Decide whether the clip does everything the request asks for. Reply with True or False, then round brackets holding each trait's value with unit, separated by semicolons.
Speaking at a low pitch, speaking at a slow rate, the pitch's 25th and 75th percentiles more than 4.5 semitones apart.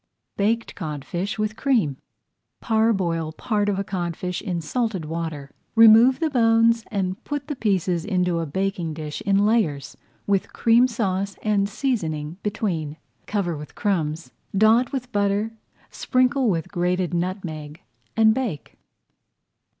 False (195 Hz; 130 wpm; 5.1 semitones)